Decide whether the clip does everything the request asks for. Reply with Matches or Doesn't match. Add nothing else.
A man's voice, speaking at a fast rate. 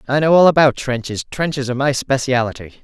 Doesn't match